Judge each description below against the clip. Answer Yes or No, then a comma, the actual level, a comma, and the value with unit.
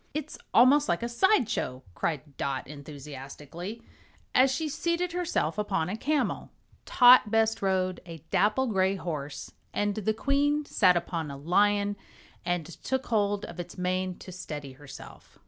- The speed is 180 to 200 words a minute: No, average, 145 wpm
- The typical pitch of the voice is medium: No, high, 195 Hz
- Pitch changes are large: Yes, wide, 6.7 semitones